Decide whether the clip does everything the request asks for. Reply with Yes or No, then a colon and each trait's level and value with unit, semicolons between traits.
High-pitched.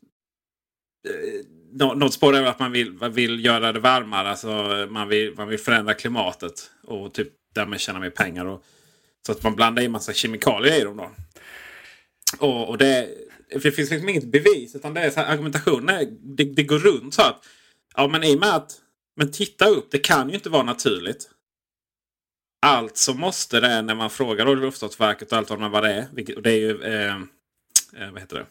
No: low, 130 Hz